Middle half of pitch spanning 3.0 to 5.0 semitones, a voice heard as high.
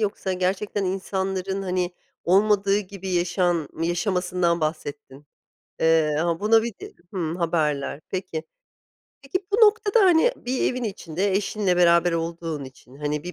No: average, 3.4 semitones; medium, 180 Hz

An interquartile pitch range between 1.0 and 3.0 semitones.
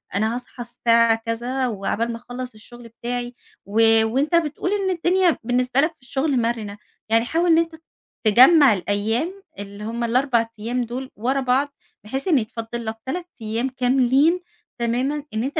No: average, 3.6 semitones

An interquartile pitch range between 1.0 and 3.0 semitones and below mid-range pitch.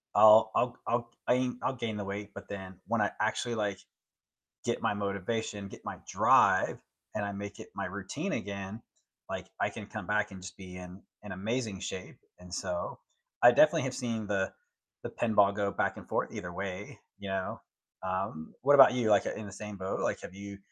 Yes: average, 2.7 semitones; low, 100 Hz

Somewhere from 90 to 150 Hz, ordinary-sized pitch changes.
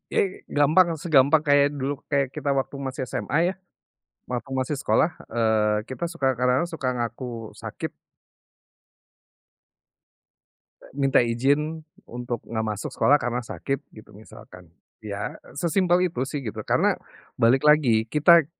Yes: low, 135 Hz; average, 4.2 semitones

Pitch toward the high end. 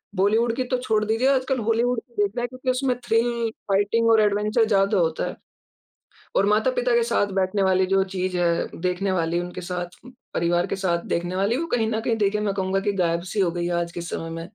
Yes: high, 200 Hz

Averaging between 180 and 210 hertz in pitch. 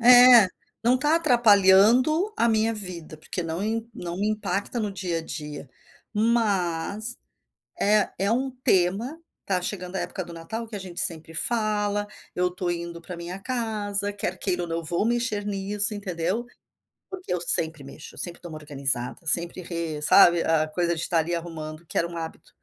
Yes: high, 190 Hz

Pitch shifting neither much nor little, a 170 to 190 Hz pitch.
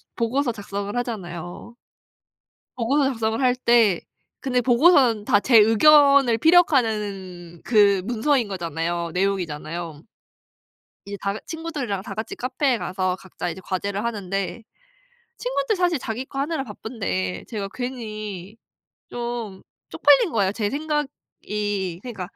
No: average, 5.0 semitones; high, 220 Hz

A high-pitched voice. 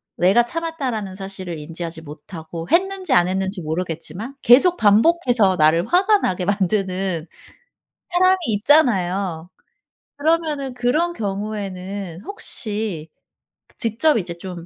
Yes: high, 200 Hz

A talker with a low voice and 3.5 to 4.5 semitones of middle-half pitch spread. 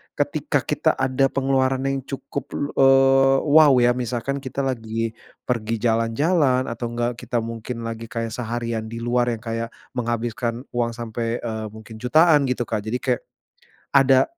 No: low, 120 Hz; average, 2.7 semitones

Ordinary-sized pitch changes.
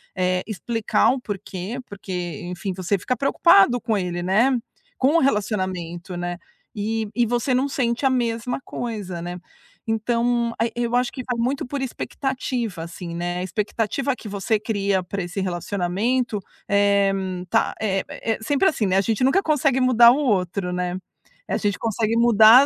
Yes: average, 4.7 semitones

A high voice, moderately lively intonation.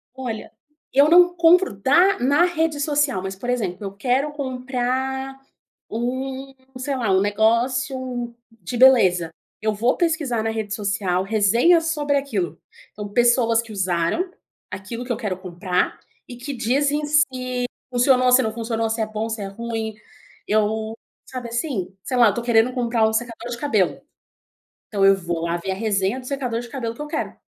Yes: high, 240 Hz; average, 3.9 semitones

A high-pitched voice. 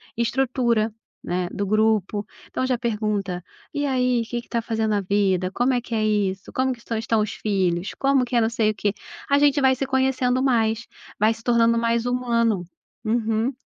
Yes: high, 230 Hz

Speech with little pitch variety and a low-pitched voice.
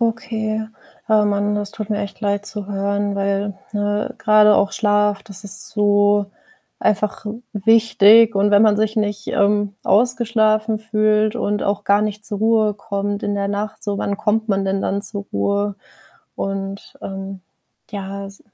No: narrow, 1.2 semitones; high, 205 Hz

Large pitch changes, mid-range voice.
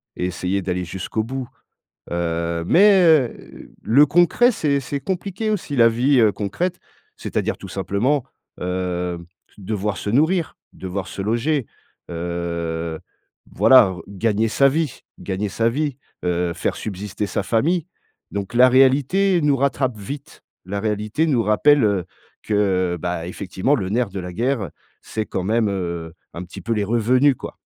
No: wide, 6.9 semitones; low, 110 Hz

